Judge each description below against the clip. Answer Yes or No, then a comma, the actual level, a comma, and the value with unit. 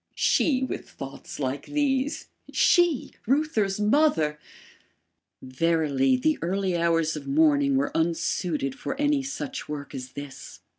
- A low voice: No, medium, 165 Hz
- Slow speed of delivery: Yes, slow, 120 wpm